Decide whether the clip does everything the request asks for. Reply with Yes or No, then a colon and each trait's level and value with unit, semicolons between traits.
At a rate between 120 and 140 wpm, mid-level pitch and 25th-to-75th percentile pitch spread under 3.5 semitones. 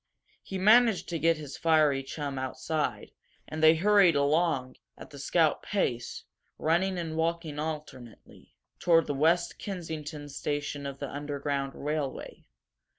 Yes: slow, 135 wpm; medium, 155 Hz; average, 2.9 semitones